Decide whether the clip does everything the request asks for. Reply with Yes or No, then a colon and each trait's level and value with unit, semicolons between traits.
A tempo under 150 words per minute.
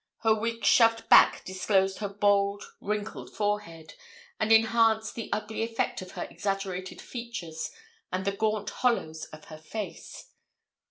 Yes: average, 140 wpm